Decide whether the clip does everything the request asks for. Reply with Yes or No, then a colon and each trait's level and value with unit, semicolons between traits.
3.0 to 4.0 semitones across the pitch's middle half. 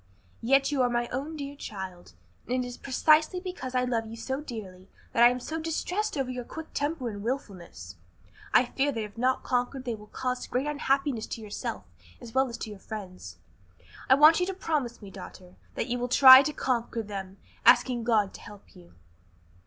No: average, 4.5 semitones